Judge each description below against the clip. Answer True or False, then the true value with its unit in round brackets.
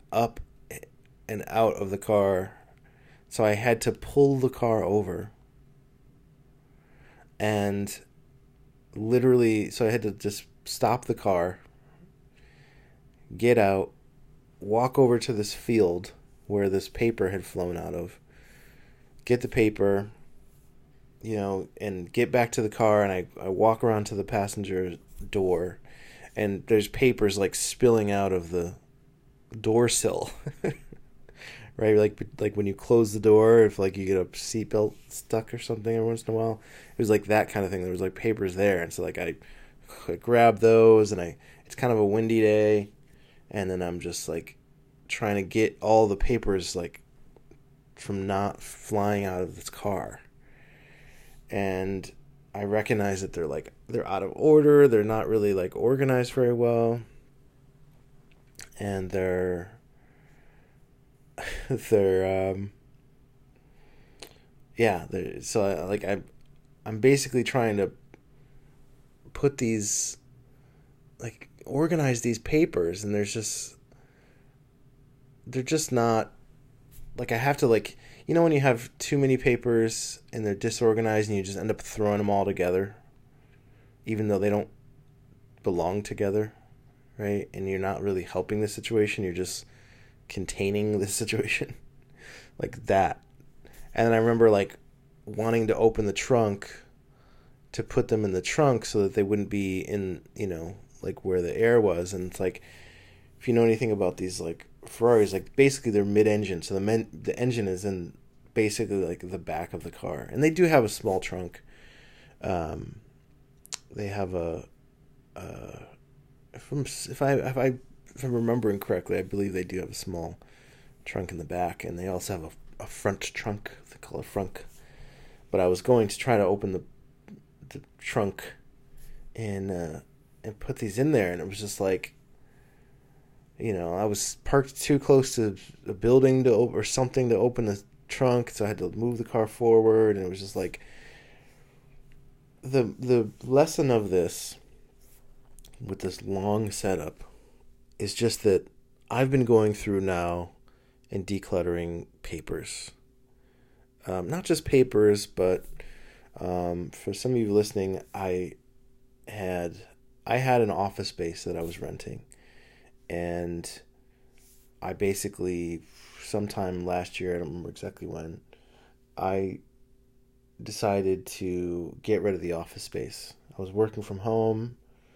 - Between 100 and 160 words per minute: True (150 wpm)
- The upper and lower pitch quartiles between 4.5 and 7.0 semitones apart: True (5.0 semitones)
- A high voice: False (115 Hz)